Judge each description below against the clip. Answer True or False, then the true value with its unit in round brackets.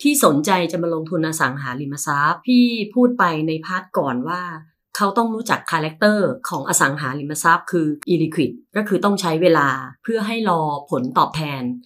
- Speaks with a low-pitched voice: False (170 Hz)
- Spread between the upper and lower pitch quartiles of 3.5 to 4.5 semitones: False (5.6 semitones)